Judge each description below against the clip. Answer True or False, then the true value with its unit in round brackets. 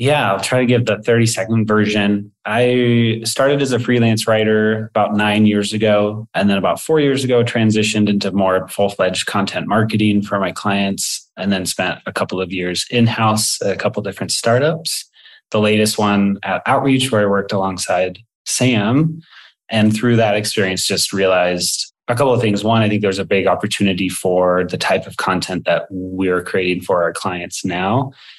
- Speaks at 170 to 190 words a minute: True (180 wpm)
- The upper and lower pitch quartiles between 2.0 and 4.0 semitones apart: True (2.9 semitones)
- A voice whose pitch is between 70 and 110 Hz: True (105 Hz)